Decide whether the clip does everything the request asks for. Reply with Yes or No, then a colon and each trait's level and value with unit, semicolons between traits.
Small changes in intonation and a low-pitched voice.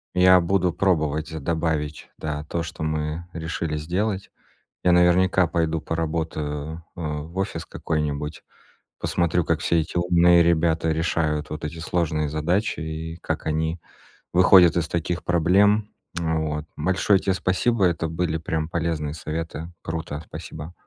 Yes: narrow, 2.1 semitones; very low, 80 Hz